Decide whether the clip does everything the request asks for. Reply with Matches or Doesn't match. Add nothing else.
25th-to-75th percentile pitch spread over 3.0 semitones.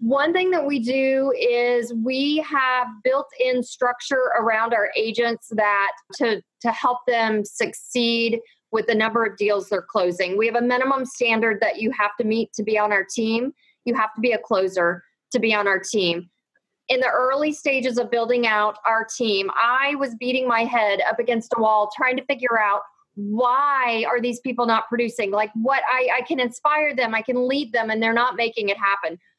Doesn't match